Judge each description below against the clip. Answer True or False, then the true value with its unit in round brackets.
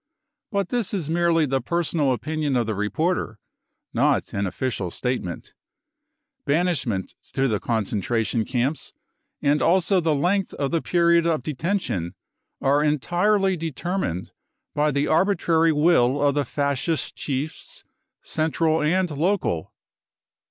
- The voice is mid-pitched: True (150 Hz)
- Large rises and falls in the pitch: False (5.0 semitones)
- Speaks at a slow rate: True (125 wpm)